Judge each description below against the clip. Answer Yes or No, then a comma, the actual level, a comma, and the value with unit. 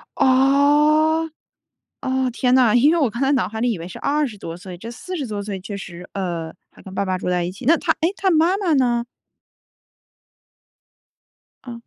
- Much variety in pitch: Yes, wide, 6.9 semitones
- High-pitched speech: Yes, high, 245 Hz